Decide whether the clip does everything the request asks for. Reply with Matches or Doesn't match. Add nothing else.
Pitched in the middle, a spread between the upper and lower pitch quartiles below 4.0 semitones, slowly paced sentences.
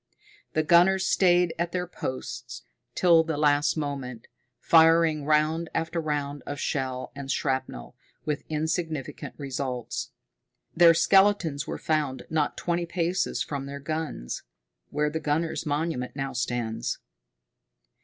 Matches